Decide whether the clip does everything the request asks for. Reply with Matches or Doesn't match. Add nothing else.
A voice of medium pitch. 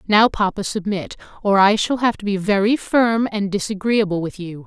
Doesn't match